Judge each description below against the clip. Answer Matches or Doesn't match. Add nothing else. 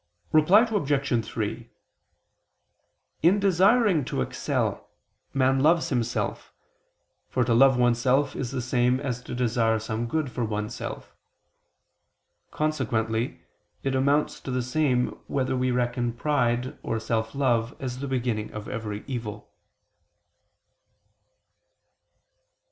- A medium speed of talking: Doesn't match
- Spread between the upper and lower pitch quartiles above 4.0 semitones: Doesn't match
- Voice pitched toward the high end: Doesn't match